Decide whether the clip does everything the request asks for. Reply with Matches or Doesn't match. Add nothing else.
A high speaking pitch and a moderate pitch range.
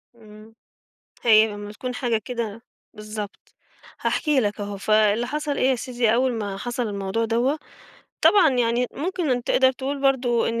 Matches